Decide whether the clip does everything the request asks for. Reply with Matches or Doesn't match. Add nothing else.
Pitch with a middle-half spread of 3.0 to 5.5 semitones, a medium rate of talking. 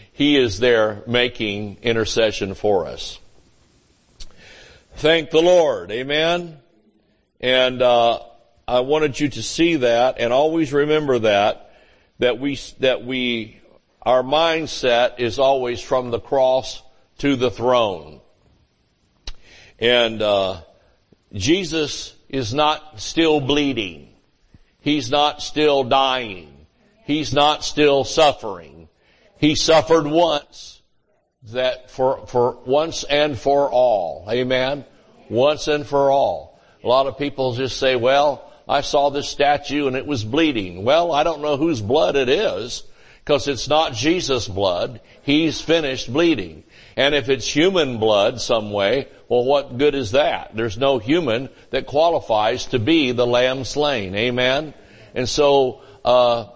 Doesn't match